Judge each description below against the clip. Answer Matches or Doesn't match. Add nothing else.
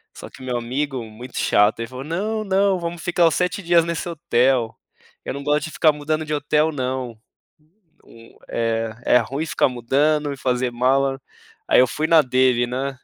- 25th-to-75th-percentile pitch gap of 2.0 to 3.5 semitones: Doesn't match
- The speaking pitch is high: Doesn't match